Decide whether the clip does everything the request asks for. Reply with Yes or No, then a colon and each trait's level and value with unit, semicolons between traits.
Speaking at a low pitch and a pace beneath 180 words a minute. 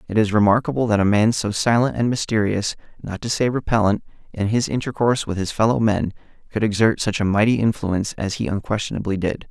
No: low, 110 Hz; average, 195 wpm